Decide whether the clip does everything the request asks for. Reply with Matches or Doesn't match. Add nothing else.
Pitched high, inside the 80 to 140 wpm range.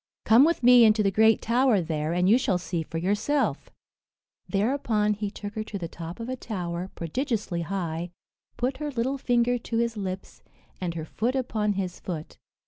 Doesn't match